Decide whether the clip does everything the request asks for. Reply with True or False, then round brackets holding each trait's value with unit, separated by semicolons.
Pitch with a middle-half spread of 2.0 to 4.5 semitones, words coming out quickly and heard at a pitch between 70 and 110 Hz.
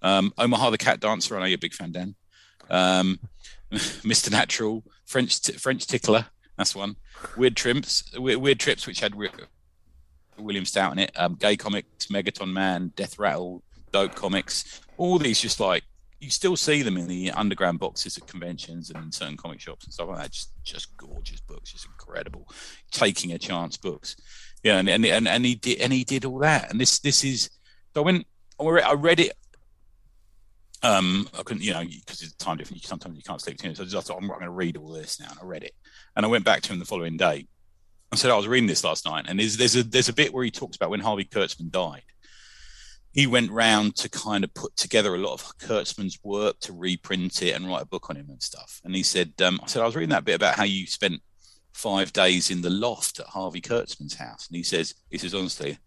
False (5.3 semitones; 230 wpm; 95 Hz)